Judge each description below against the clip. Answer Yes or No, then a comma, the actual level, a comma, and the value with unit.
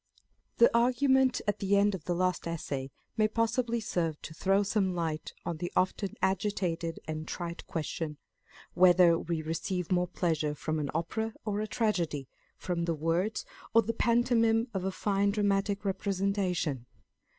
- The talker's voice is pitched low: No, medium, 185 Hz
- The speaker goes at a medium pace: Yes, average, 155 wpm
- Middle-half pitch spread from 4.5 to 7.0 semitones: No, average, 4.1 semitones